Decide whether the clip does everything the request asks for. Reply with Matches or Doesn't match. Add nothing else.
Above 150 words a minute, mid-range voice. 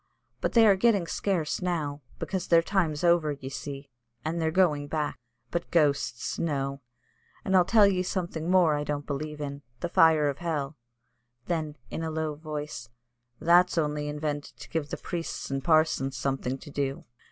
Matches